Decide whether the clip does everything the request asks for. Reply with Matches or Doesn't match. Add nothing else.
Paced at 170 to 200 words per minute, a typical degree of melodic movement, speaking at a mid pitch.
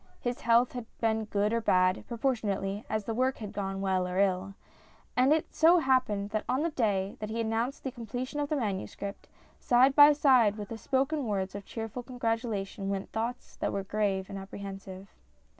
Doesn't match